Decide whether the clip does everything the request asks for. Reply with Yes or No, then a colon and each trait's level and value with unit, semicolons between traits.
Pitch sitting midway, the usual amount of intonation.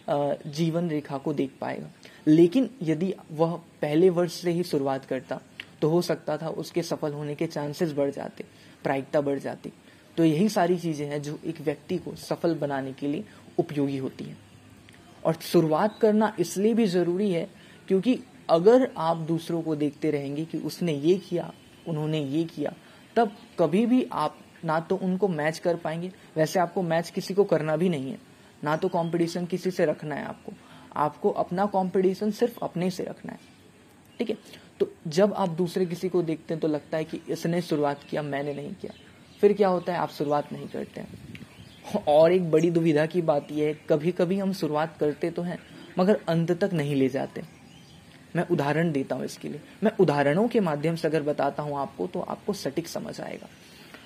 Yes: medium, 165 Hz; average, 3.4 semitones